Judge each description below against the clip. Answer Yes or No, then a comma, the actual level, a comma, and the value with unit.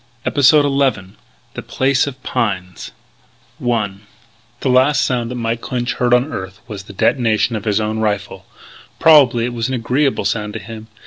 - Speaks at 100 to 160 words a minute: No, average, 170 wpm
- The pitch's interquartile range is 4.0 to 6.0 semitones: No, average, 3.6 semitones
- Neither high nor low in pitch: No, low, 115 Hz